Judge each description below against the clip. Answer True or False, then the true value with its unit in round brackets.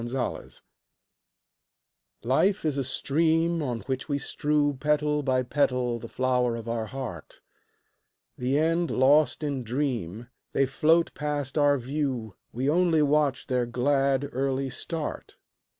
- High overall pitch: False (135 Hz)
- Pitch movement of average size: True (3.1 semitones)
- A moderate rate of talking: False (130 wpm)